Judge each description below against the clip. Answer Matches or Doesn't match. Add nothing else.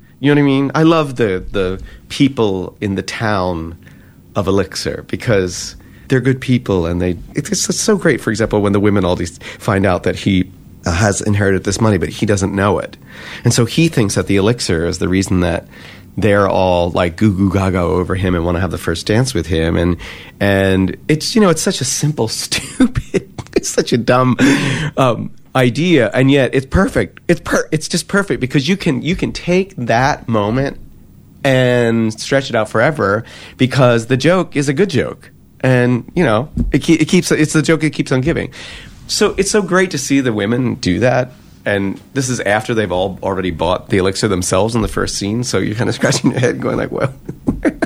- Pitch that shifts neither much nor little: Doesn't match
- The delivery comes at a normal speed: Doesn't match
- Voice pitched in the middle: Doesn't match